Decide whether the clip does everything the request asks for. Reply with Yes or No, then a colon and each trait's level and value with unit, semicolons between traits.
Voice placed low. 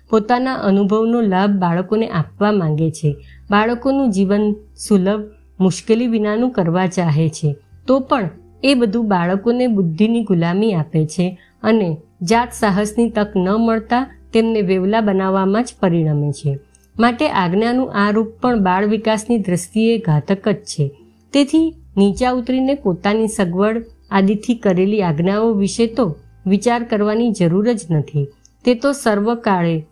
No: high, 210 Hz